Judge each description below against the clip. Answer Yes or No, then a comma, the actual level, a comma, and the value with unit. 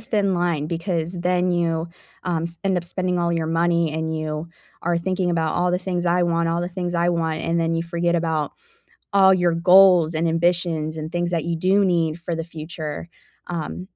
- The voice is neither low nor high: Yes, medium, 170 Hz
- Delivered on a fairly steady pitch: Yes, narrow, 1.5 semitones